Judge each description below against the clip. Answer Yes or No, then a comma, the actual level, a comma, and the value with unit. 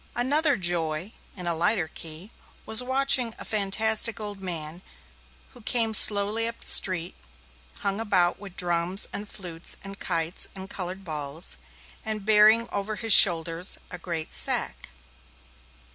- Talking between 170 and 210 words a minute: No, average, 140 wpm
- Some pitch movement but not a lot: Yes, average, 4.2 semitones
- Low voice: No, high, 195 Hz